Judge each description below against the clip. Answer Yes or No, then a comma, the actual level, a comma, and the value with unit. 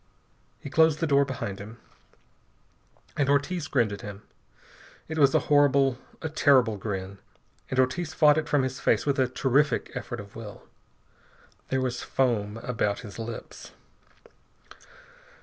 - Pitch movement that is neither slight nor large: Yes, average, 4.3 semitones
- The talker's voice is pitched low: Yes, low, 130 Hz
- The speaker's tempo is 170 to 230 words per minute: No, average, 145 wpm